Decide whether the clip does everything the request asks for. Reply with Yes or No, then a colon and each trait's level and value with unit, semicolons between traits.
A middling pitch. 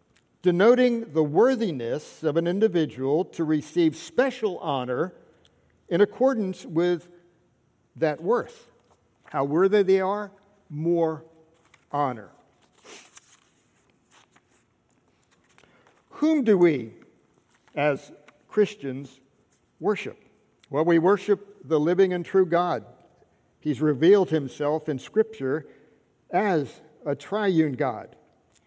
Yes: medium, 170 Hz